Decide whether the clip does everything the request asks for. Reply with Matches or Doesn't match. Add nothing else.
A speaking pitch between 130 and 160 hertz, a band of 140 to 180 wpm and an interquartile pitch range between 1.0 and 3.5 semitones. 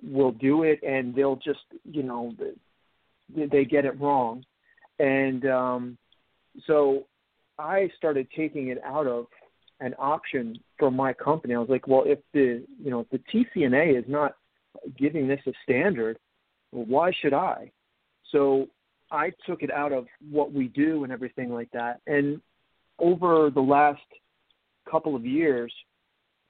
Matches